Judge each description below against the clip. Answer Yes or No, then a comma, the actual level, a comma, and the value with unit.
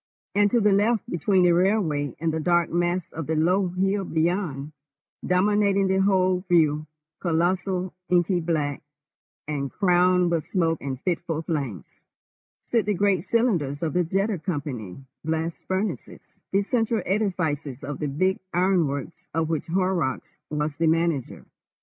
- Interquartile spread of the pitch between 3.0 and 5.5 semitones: Yes, average, 3.6 semitones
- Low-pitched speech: No, medium, 175 Hz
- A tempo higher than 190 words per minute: No, average, 145 wpm